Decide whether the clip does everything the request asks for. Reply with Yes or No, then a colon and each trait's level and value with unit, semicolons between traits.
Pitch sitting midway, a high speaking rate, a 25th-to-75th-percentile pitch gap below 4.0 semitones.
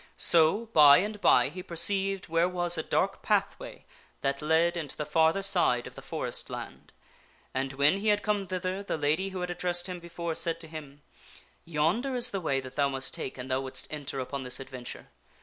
No: medium, 165 Hz; fast, 210 wpm; average, 4.6 semitones